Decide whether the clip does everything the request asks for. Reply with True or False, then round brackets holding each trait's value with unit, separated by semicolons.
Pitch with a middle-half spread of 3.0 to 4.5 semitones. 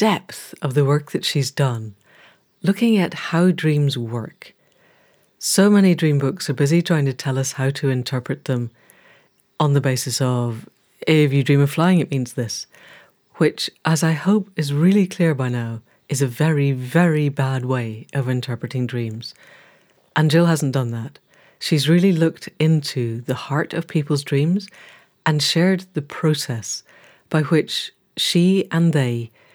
True (4.2 semitones)